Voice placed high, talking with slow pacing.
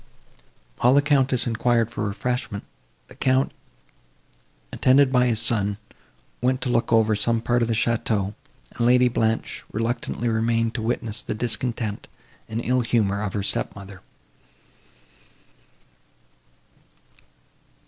No: low, 115 Hz; slow, 125 wpm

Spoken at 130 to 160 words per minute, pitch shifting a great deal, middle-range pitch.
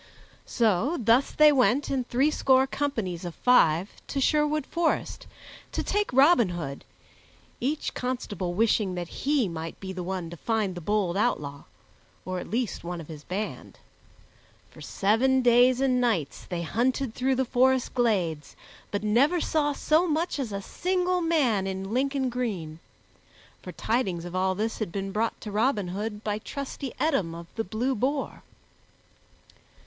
No: average, 155 wpm; wide, 6.2 semitones; high, 230 Hz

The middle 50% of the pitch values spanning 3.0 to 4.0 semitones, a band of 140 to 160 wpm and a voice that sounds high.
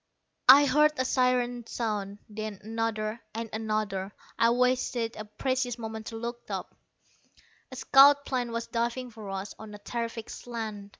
No: narrow, 2.5 semitones; average, 155 wpm; high, 230 Hz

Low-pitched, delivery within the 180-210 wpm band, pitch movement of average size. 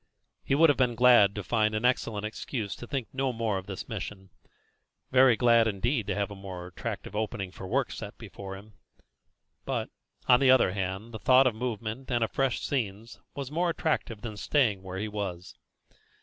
Yes: low, 110 Hz; average, 190 wpm; average, 4.0 semitones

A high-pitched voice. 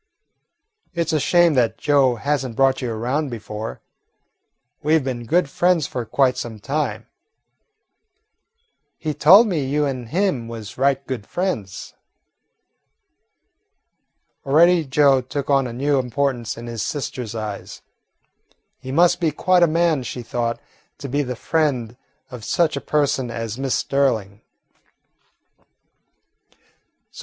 No: low, 135 Hz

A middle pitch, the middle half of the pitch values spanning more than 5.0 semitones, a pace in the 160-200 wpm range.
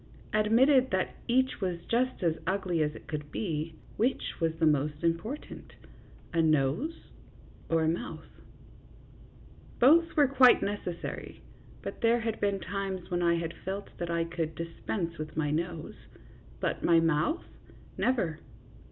No: medium, 175 Hz; wide, 5.6 semitones; average, 145 wpm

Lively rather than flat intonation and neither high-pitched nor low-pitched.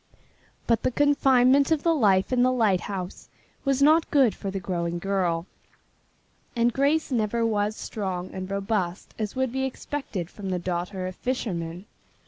No: wide, 5.8 semitones; high, 210 Hz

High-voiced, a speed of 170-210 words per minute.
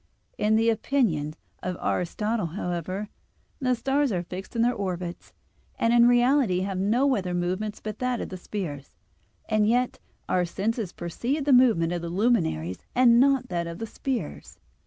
Yes: high, 210 Hz; average, 175 wpm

